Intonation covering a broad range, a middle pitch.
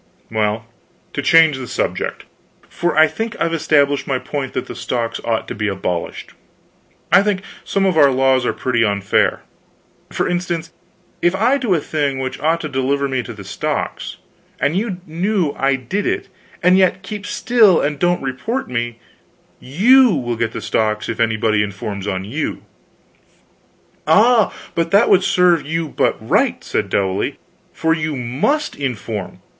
Yes: wide, 7.3 semitones; medium, 145 Hz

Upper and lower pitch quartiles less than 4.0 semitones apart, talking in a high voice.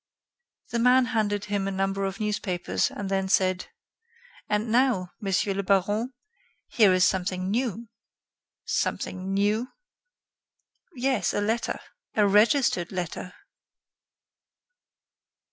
Yes: average, 2.9 semitones; high, 205 Hz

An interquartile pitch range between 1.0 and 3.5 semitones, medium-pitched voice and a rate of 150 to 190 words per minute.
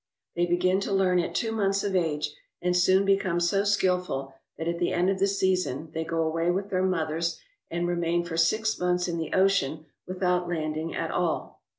No: narrow, 2.4 semitones; medium, 180 Hz; average, 200 wpm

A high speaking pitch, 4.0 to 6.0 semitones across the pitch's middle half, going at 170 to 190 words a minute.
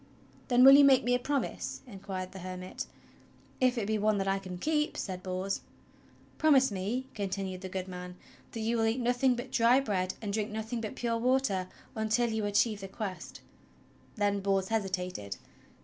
Yes: high, 215 Hz; average, 4.3 semitones; average, 180 wpm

